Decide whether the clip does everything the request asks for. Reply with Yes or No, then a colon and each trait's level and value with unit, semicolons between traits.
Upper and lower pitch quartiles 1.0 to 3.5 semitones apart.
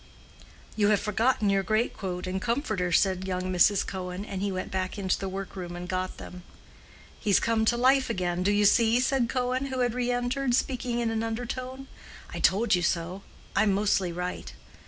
No: average, 4.6 semitones